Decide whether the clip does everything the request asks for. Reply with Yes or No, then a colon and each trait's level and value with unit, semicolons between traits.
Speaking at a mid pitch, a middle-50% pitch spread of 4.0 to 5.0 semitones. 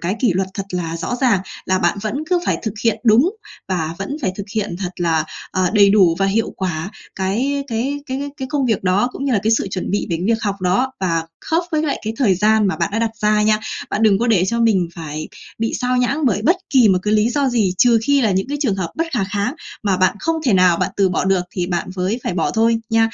No: high, 210 Hz; average, 4.6 semitones